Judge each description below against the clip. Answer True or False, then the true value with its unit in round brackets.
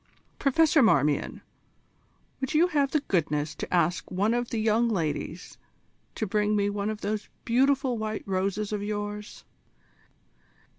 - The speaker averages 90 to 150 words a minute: True (140 wpm)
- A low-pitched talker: False (210 Hz)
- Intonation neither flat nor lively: True (3.8 semitones)